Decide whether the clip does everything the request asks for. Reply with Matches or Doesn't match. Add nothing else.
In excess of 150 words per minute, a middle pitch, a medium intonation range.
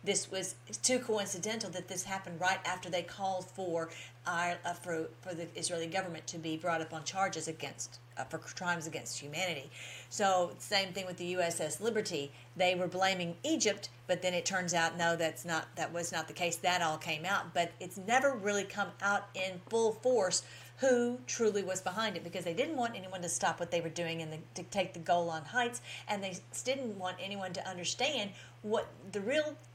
Matches